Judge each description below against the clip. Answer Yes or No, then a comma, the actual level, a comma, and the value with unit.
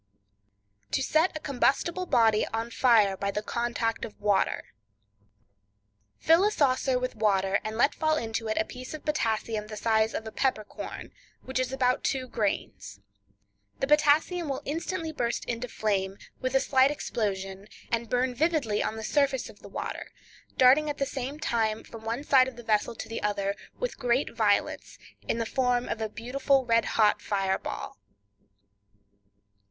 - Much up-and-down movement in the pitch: No, average, 4.2 semitones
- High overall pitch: Yes, high, 235 Hz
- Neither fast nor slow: Yes, average, 170 wpm